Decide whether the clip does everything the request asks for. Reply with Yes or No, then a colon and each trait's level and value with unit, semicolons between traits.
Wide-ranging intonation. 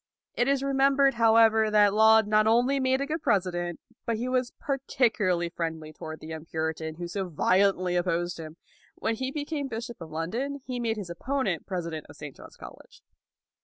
Yes: wide, 6.9 semitones